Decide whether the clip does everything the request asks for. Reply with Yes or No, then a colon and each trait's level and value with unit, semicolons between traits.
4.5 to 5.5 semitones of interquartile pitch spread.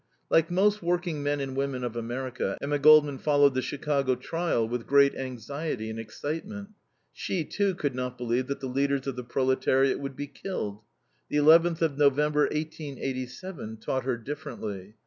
No: average, 3.3 semitones